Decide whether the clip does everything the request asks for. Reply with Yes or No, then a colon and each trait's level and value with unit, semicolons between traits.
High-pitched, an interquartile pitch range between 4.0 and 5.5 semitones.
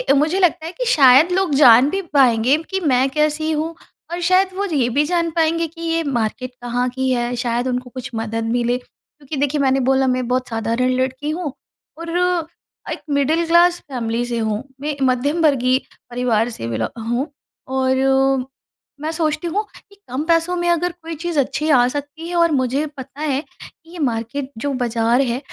Yes: very high, 275 Hz; average, 4.5 semitones